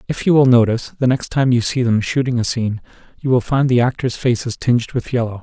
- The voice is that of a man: Yes, male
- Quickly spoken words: Yes, fast, 245 wpm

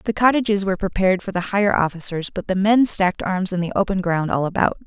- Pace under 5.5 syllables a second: No, 6.5 syllables/s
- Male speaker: No, female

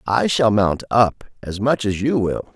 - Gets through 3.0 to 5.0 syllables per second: Yes, 4.0 syllables/s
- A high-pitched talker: No, low, 110 Hz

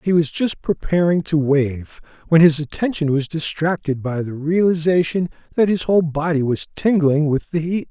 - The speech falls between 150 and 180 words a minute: Yes, average, 175 wpm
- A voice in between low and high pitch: Yes, medium, 160 Hz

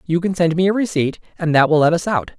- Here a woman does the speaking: No, male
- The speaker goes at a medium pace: No, fast, 300 wpm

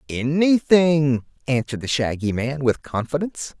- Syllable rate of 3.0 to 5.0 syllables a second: Yes, 4.7 syllables/s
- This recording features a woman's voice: No, male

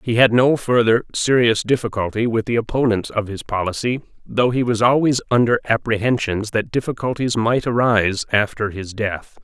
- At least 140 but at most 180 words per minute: Yes, average, 160 wpm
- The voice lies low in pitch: Yes, low, 115 Hz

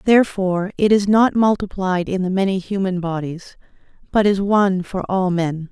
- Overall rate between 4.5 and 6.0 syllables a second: Yes, 5.0 syllables/s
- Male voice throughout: No, female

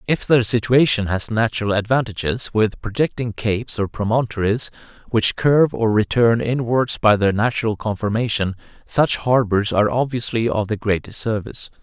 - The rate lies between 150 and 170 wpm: No, average, 140 wpm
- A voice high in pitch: No, low, 110 Hz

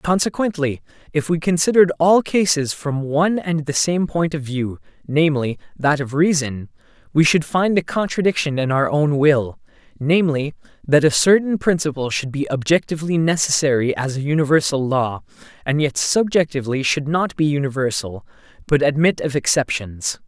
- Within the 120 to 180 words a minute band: Yes, average, 150 wpm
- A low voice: No, medium, 150 Hz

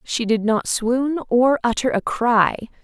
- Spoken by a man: No, female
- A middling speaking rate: Yes, average, 170 wpm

